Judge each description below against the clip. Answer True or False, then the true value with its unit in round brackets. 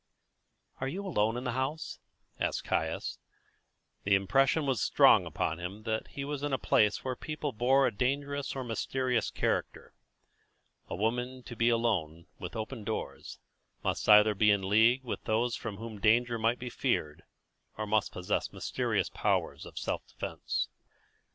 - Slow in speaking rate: False (165 wpm)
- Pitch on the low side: True (115 Hz)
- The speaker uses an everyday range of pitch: True (3.8 semitones)